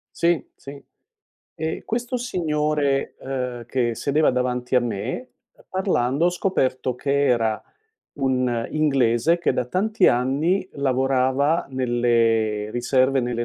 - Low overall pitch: Yes, low, 130 Hz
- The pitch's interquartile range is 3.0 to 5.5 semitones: Yes, average, 4.0 semitones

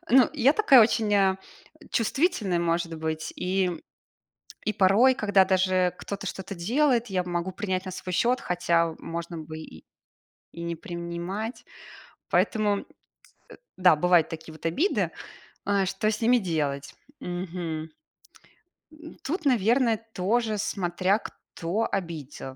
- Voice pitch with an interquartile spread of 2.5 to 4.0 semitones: No, average, 4.4 semitones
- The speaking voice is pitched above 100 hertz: Yes, high, 190 Hz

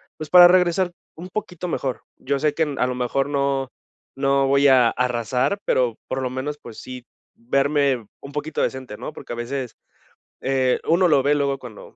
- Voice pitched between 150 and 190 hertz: No, low, 135 Hz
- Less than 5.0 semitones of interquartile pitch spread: Yes, average, 2.7 semitones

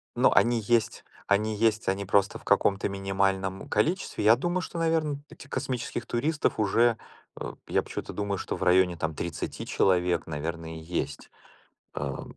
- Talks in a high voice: No, low, 100 Hz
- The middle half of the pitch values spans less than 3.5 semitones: No, average, 4.5 semitones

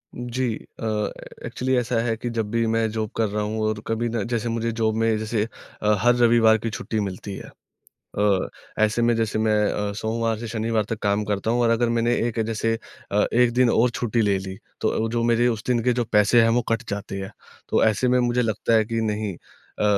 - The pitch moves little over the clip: Yes, narrow, 1.7 semitones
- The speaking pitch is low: Yes, low, 115 Hz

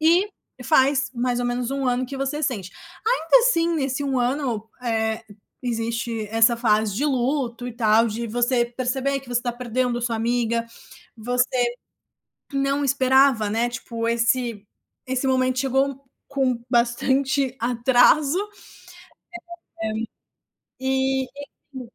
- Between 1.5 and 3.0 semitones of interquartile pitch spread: Yes, narrow, 2.4 semitones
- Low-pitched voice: No, very high, 250 Hz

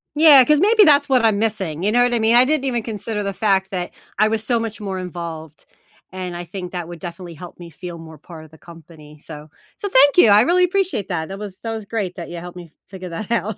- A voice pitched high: Yes, high, 195 Hz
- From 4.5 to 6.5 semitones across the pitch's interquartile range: Yes, average, 5.1 semitones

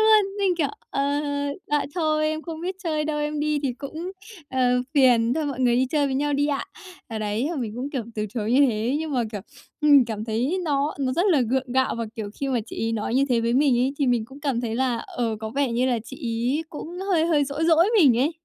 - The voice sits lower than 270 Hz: No, very high, 275 Hz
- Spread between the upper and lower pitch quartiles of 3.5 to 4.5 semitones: Yes, average, 4.2 semitones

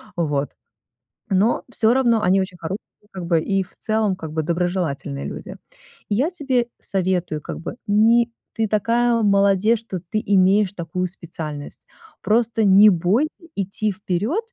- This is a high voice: Yes, high, 195 Hz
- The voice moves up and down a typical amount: Yes, average, 3.8 semitones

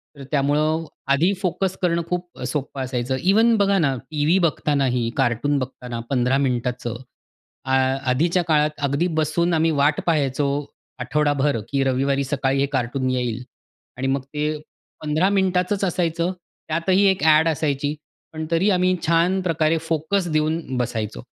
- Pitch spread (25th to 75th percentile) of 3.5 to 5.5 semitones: Yes, average, 4.1 semitones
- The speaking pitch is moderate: Yes, medium, 150 Hz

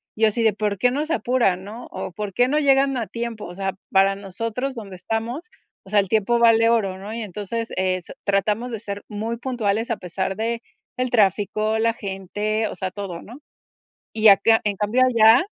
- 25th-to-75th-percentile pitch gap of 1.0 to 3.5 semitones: Yes, average, 2.9 semitones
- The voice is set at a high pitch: Yes, high, 215 Hz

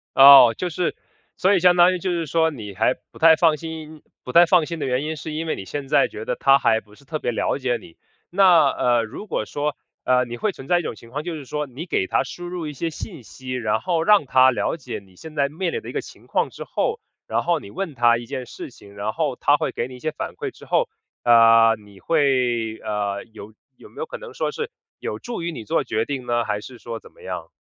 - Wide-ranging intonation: Yes, wide, 5.8 semitones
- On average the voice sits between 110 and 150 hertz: Yes, medium, 140 Hz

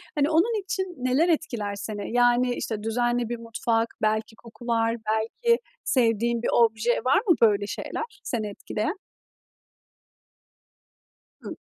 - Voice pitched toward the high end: Yes, high, 235 Hz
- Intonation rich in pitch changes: No, average, 4.2 semitones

